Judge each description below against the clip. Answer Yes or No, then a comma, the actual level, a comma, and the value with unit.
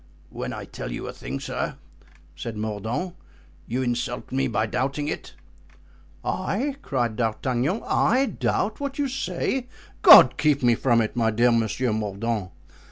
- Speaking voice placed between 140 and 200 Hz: No, low, 120 Hz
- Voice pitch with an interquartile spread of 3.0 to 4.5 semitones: No, average, 5.2 semitones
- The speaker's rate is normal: Yes, average, 150 wpm